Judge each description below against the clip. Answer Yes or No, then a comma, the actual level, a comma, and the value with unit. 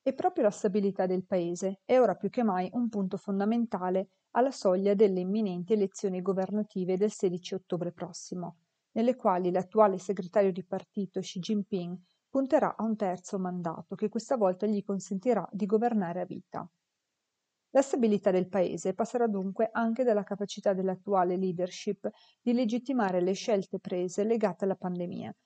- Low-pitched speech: No, high, 200 Hz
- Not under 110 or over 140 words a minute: No, average, 155 wpm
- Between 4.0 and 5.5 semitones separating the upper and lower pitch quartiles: No, average, 2.9 semitones